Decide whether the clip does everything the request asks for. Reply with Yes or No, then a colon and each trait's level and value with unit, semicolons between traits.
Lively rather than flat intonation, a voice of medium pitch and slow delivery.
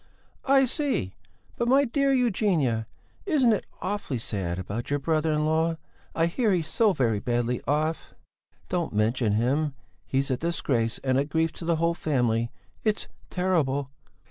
No: wide, 7.3 semitones; medium, 155 Hz; average, 155 wpm